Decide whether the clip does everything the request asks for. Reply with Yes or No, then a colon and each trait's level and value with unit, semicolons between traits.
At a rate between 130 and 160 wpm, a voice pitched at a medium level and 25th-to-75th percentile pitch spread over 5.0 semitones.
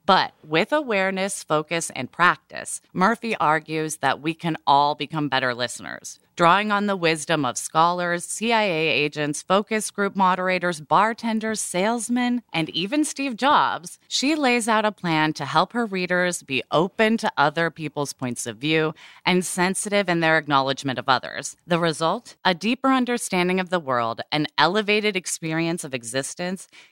Yes: average, 155 wpm; medium, 175 Hz; wide, 5.5 semitones